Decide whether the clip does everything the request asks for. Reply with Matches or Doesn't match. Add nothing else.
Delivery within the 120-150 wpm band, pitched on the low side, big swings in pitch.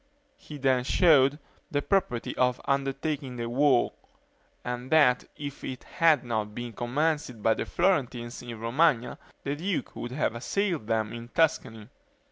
Doesn't match